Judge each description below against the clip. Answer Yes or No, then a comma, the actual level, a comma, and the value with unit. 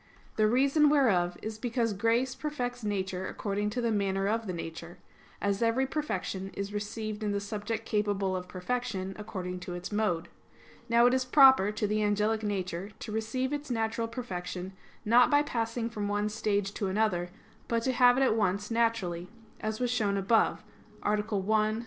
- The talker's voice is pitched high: Yes, high, 215 Hz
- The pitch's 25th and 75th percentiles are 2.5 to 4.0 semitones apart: Yes, average, 3.0 semitones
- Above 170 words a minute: Yes, average, 180 wpm